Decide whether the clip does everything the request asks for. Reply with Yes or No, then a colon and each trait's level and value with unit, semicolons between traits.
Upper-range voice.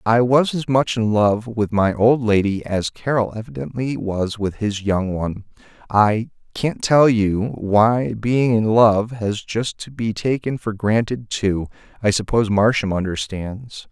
No: low, 110 Hz